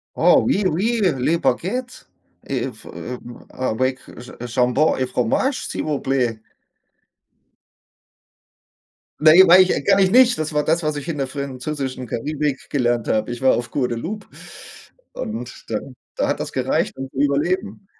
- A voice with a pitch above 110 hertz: Yes, medium, 140 Hz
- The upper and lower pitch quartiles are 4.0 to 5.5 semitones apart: Yes, average, 5.2 semitones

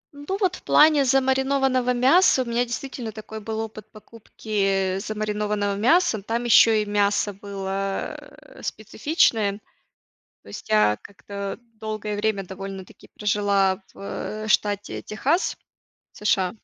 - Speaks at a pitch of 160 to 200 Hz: No, high, 215 Hz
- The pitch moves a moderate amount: Yes, average, 3.4 semitones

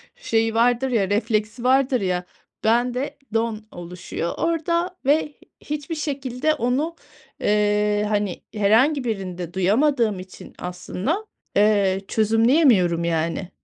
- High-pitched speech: Yes, high, 225 Hz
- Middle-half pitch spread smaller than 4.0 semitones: No, wide, 5.6 semitones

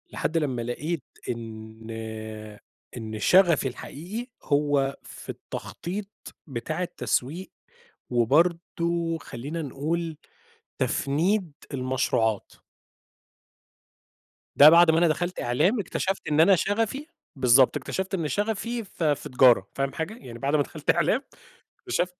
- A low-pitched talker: No, medium, 155 Hz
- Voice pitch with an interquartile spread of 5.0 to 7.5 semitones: Yes, wide, 5.6 semitones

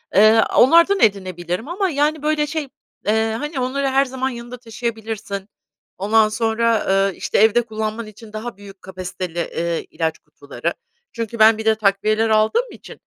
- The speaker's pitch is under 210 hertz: No, high, 220 Hz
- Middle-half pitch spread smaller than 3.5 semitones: No, average, 3.9 semitones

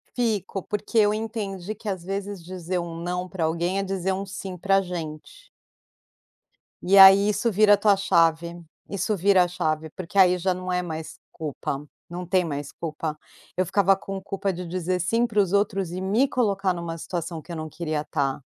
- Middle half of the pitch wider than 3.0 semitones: No, average, 2.7 semitones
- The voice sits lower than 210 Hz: Yes, medium, 185 Hz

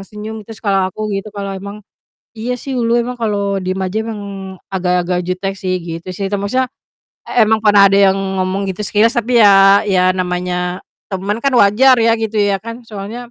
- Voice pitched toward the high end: Yes, high, 200 Hz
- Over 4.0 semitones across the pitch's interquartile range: No, average, 2.7 semitones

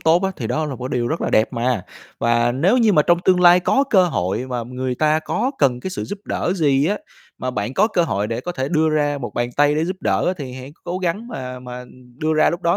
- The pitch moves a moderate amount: No, wide, 5.8 semitones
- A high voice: No, medium, 150 Hz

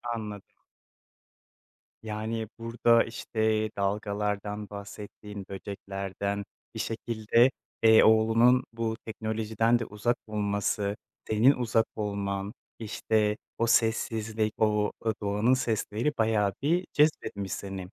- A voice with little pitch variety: Yes, narrow, 1.9 semitones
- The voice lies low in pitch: Yes, low, 110 Hz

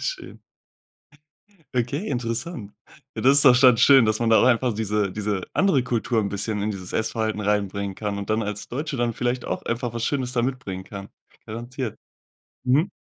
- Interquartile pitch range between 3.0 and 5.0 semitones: Yes, average, 3.4 semitones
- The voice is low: Yes, low, 115 Hz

